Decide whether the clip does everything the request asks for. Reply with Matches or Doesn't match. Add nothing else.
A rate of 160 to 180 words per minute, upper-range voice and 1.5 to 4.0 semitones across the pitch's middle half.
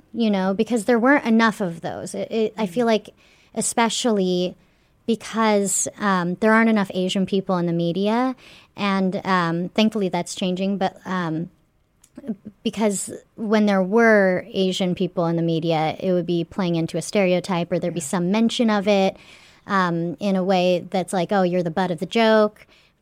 Matches